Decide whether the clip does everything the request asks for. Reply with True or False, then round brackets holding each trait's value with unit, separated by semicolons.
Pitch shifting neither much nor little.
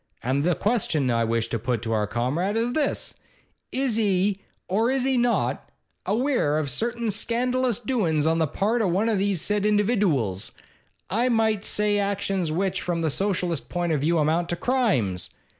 False (6.6 semitones)